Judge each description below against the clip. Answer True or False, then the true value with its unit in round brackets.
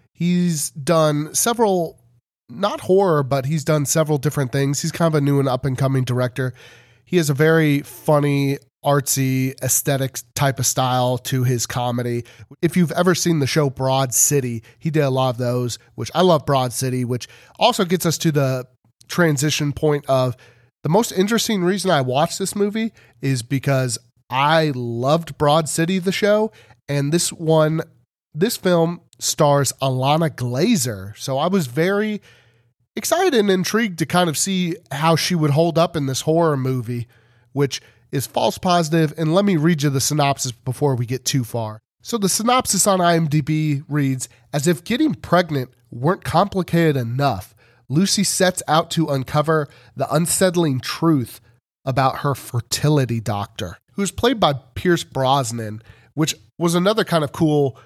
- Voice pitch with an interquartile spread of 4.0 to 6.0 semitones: True (5.1 semitones)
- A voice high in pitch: False (145 Hz)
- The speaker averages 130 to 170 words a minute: True (165 wpm)